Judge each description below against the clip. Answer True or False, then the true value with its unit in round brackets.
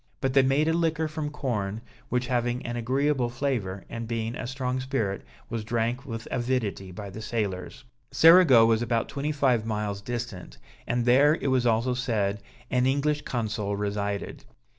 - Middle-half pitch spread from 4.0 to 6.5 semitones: False (3.4 semitones)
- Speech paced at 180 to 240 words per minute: False (165 wpm)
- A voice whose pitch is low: True (120 Hz)